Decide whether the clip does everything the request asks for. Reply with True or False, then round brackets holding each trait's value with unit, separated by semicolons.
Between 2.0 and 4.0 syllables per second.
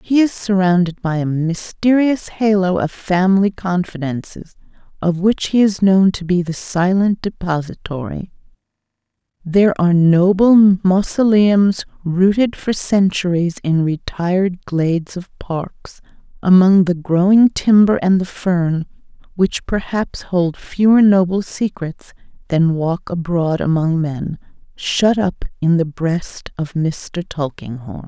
True (3.9 syllables/s)